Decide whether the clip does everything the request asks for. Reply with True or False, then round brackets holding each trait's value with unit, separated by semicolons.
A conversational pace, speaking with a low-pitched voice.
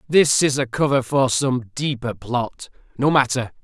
True (165 wpm; 130 Hz)